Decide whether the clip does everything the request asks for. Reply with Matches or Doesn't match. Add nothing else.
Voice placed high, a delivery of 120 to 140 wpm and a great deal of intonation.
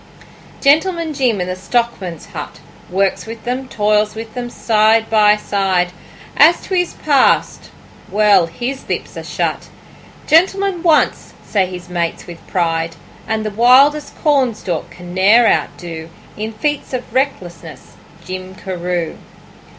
Matches